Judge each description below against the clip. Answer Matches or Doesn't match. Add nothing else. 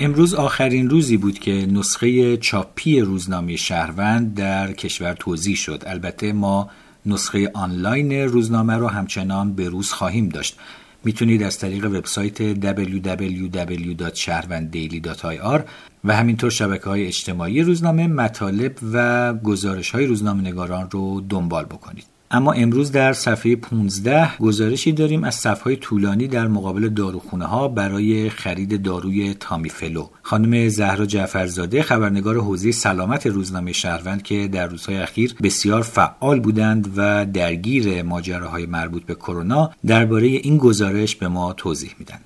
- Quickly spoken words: Doesn't match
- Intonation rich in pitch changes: Doesn't match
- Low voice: Matches